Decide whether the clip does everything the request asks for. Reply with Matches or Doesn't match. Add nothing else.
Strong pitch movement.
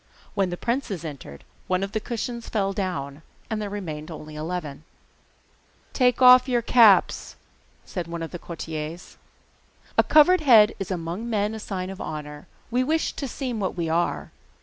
Matches